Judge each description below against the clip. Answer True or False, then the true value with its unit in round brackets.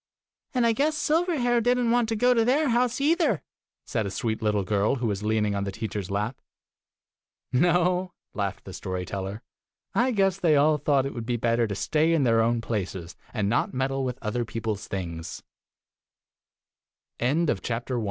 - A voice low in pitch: True (130 Hz)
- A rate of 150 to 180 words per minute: True (170 wpm)